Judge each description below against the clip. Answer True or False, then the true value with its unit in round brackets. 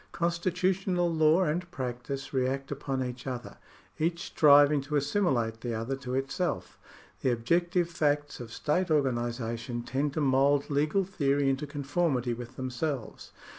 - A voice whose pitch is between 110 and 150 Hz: True (140 Hz)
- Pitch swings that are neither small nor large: True (4.5 semitones)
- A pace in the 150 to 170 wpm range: False (140 wpm)